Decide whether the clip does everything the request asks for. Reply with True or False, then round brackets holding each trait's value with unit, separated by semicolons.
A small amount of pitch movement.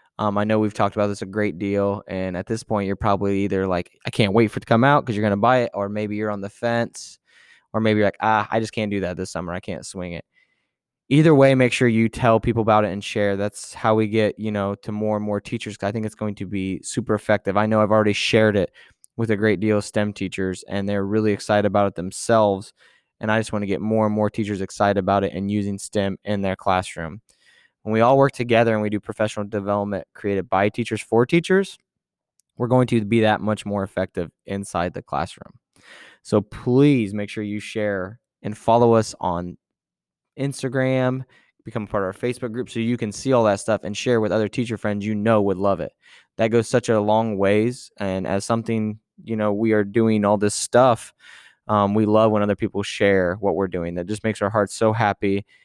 True (2.1 semitones)